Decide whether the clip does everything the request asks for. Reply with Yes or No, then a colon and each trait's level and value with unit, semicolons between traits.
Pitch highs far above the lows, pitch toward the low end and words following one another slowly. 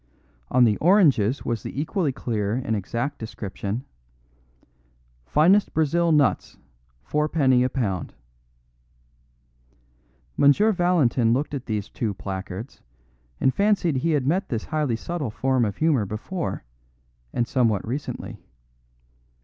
Yes: wide, 5.9 semitones; low, 130 Hz; slow, 120 wpm